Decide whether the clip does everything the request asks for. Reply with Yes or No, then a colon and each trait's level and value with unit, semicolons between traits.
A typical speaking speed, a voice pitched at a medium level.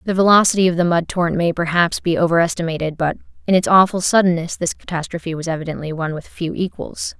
Yes: average, 190 wpm; medium, 170 Hz